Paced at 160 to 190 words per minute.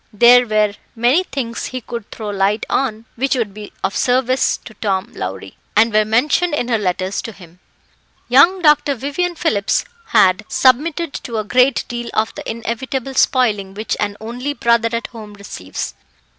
Yes: average, 170 wpm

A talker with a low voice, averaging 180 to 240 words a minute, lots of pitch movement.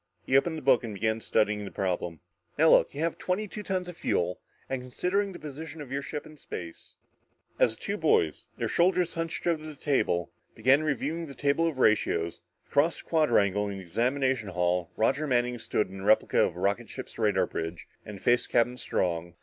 Yes: low, 125 Hz; fast, 205 wpm; wide, 7.7 semitones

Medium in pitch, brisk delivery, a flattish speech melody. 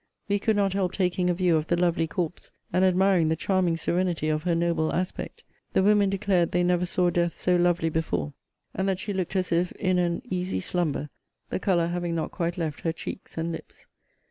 Yes: medium, 175 Hz; fast, 210 wpm; narrow, 1.8 semitones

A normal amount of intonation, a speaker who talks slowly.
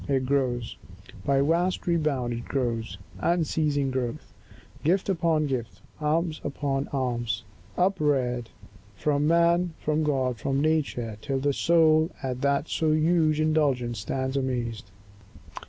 Yes: average, 3.8 semitones; slow, 120 wpm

